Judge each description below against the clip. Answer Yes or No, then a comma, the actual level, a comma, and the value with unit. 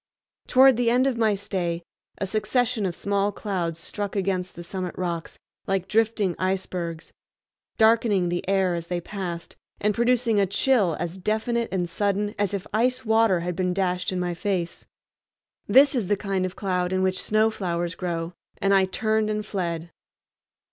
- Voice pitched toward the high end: Yes, high, 195 Hz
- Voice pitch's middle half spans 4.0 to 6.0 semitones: No, average, 3.3 semitones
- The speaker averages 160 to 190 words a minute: Yes, average, 170 wpm